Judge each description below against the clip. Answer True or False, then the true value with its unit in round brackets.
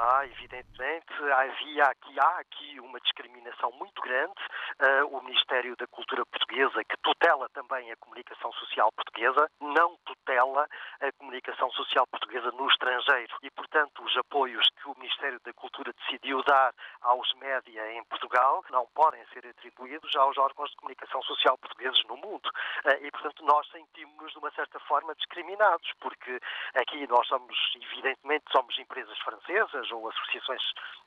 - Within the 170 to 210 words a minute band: False (145 wpm)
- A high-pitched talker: False (140 Hz)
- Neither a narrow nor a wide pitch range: True (5.0 semitones)